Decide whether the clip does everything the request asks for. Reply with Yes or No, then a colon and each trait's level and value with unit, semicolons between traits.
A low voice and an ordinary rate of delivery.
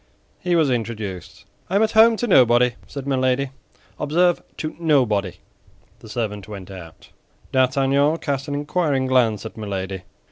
Yes: low, 130 Hz; average, 145 wpm